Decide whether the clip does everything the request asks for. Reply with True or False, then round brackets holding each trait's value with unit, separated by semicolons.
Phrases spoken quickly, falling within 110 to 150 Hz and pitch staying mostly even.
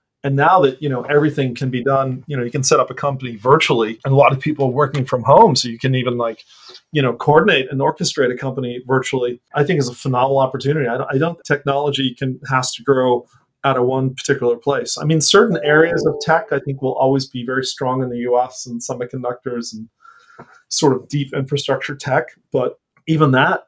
True (220 wpm; 135 Hz; 2.1 semitones)